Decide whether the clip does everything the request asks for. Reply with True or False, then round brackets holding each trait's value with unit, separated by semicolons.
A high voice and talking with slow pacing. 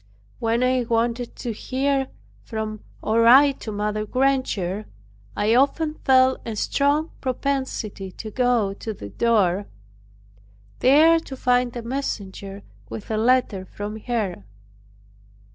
True (235 Hz; 125 wpm)